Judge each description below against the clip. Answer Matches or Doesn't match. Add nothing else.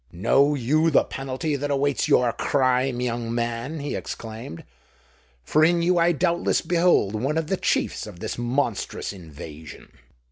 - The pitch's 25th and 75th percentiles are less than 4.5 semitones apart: Doesn't match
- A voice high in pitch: Doesn't match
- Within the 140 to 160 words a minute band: Matches